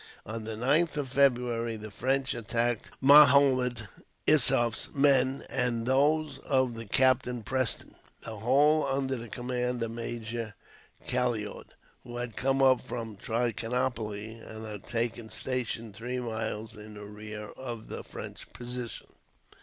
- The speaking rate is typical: No, slow, 130 wpm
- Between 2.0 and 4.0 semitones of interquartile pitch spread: Yes, average, 2.8 semitones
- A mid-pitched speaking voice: No, low, 120 Hz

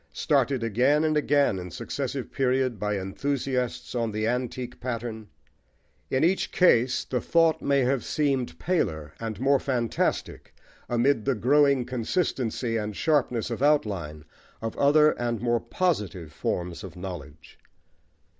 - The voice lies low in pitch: Yes, low, 120 Hz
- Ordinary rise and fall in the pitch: Yes, average, 4.7 semitones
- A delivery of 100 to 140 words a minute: Yes, slow, 135 wpm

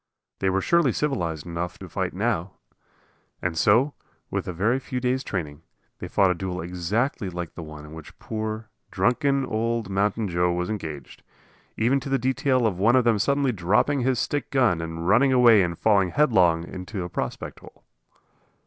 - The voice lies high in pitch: No, low, 100 Hz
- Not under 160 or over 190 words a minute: Yes, average, 180 wpm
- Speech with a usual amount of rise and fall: No, wide, 6.2 semitones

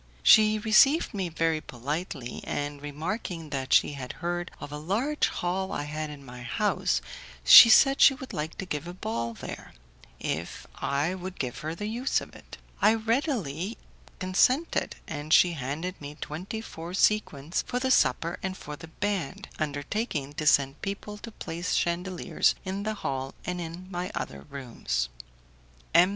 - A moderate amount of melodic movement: No, wide, 5.8 semitones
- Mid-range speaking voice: Yes, medium, 170 Hz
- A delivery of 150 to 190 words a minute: Yes, average, 165 wpm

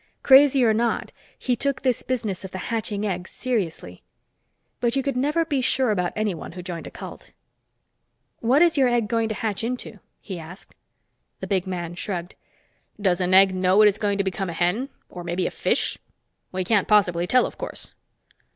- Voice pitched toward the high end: Yes, high, 205 Hz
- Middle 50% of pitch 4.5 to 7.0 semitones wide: Yes, average, 5.1 semitones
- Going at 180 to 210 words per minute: Yes, average, 190 wpm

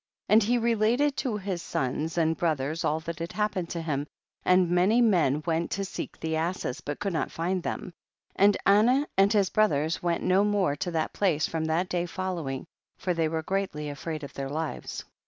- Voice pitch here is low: No, medium, 175 Hz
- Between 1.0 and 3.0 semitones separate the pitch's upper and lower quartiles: No, average, 3.9 semitones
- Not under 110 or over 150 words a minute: No, average, 200 wpm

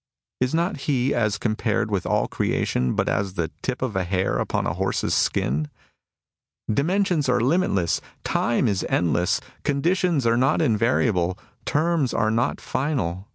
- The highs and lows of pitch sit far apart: Yes, wide, 6.9 semitones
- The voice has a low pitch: Yes, low, 115 Hz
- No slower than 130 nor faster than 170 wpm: Yes, average, 155 wpm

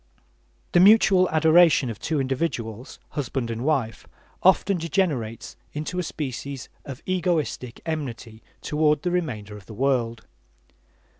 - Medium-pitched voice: Yes, medium, 145 Hz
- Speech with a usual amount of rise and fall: No, wide, 6.1 semitones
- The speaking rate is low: Yes, slow, 125 wpm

